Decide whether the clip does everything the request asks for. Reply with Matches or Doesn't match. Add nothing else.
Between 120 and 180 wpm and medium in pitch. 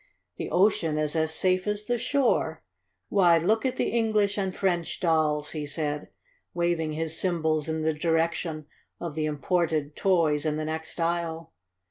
Matches